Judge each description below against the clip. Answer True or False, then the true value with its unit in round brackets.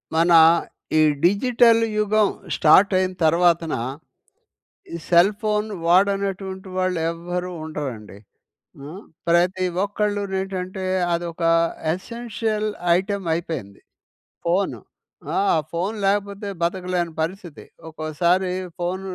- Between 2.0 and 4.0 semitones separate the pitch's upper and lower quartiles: True (2.9 semitones)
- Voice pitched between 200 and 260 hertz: False (185 Hz)